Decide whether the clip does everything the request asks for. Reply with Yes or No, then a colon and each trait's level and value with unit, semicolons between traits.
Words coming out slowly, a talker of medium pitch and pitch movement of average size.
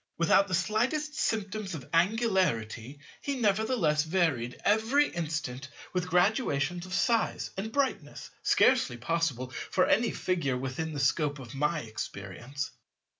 No: slow, 125 wpm; medium, 170 Hz; wide, 7.5 semitones